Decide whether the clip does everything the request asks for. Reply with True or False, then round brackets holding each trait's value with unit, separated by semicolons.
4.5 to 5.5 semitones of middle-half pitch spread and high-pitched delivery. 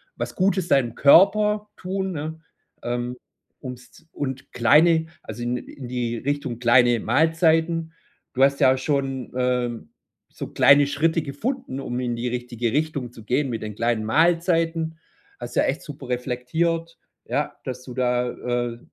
False (4.8 semitones; 135 Hz)